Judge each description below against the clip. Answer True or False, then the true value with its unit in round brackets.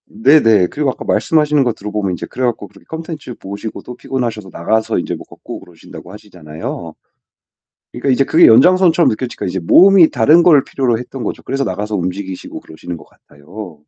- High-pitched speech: False (110 Hz)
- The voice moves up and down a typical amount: False (6.5 semitones)